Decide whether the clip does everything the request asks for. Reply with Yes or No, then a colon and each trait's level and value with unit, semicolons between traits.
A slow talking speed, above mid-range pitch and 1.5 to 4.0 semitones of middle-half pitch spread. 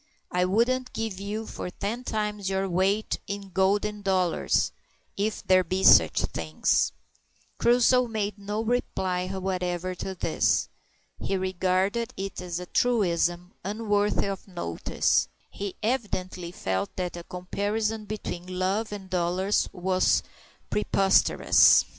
Yes: slow, 125 wpm; high, 195 Hz; narrow, 2.5 semitones